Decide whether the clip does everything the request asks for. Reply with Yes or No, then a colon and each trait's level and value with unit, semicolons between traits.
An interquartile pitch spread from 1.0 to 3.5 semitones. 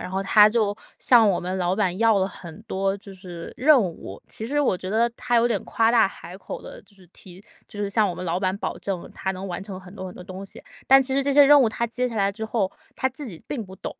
No: average, 3.9 semitones